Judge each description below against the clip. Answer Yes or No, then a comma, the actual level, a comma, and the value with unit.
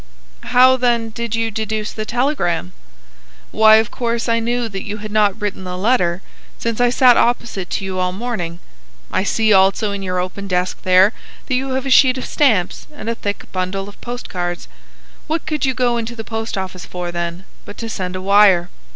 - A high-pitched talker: Yes, high, 215 Hz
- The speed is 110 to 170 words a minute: No, fast, 205 wpm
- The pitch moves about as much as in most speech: Yes, average, 4.2 semitones